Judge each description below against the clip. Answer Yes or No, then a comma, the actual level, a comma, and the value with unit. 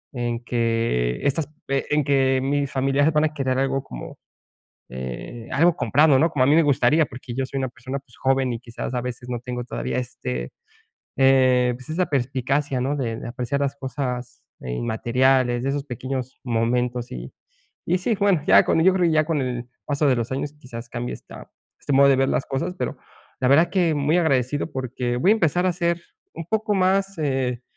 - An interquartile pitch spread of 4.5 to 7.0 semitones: No, average, 3.2 semitones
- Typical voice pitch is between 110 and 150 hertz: Yes, low, 135 Hz